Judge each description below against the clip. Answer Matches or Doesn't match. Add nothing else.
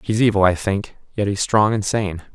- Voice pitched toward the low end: Matches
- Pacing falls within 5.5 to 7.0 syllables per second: Doesn't match